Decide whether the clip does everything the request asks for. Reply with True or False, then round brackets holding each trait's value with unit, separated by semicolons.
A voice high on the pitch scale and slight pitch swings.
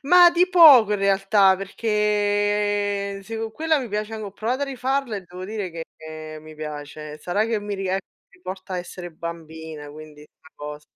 False (200 Hz; 5.3 semitones)